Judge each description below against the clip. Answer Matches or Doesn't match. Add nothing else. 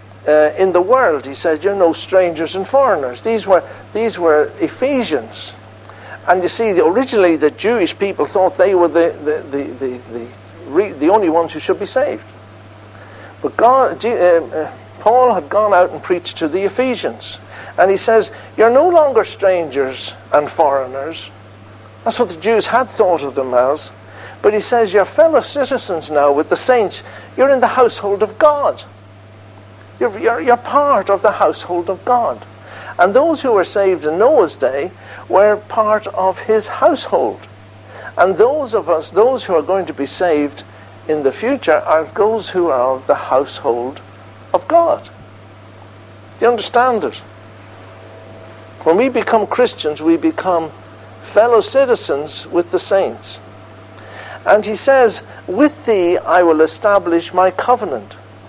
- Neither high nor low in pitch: Matches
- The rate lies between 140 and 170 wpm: Matches